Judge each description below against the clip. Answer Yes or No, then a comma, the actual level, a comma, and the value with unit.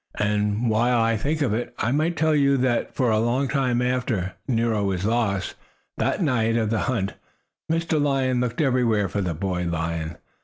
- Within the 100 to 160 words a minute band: No, average, 185 wpm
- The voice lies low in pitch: Yes, low, 115 Hz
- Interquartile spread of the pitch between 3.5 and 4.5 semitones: Yes, average, 4.0 semitones